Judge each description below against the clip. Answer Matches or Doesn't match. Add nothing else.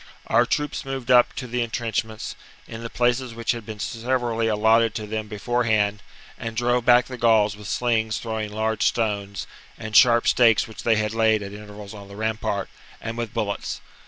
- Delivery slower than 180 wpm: Doesn't match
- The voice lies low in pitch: Matches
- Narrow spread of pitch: Matches